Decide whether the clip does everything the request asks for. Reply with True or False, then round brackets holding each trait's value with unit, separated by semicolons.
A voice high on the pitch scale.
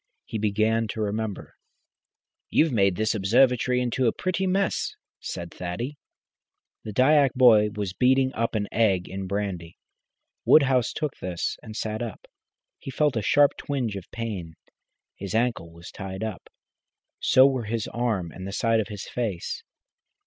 False (110 Hz)